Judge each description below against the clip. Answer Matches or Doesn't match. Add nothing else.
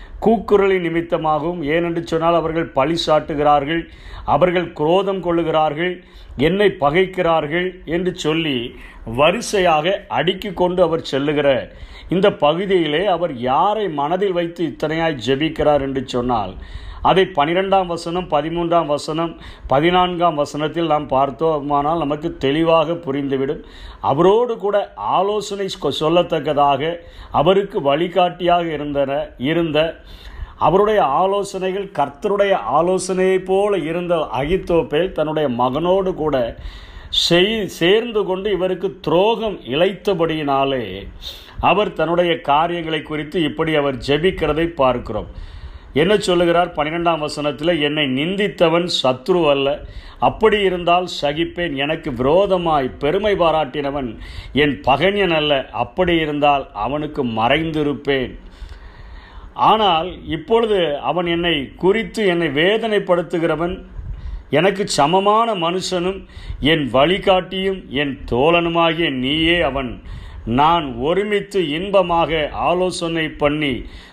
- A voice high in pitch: Doesn't match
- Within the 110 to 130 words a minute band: Doesn't match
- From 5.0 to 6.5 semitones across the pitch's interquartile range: Doesn't match